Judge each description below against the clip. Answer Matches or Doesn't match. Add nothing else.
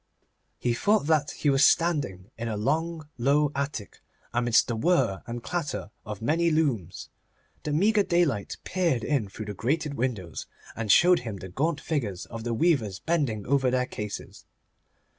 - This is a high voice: Doesn't match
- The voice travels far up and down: Matches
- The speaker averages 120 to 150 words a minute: Doesn't match